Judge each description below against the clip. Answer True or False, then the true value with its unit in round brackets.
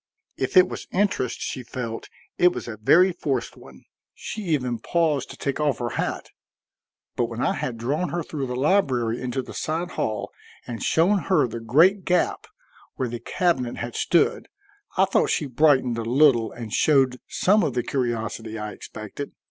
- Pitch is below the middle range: True (130 Hz)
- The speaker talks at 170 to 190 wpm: True (180 wpm)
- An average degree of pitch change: False (5.9 semitones)